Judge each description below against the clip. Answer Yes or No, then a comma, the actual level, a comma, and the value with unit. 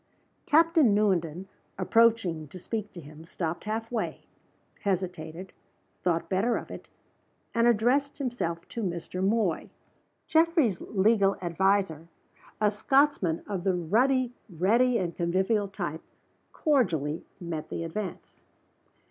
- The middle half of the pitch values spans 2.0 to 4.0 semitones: No, average, 5.3 semitones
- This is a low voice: No, high, 195 Hz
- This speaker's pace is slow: Yes, slow, 115 wpm